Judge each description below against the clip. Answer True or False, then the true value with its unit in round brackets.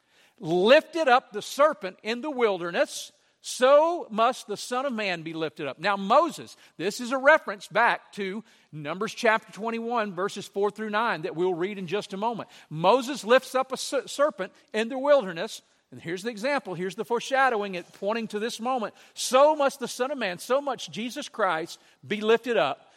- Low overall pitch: False (225 Hz)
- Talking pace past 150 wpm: True (185 wpm)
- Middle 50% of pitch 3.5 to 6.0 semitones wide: True (5.1 semitones)